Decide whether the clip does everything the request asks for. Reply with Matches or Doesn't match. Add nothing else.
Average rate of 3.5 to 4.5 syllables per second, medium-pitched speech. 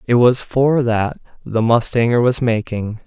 Doesn't match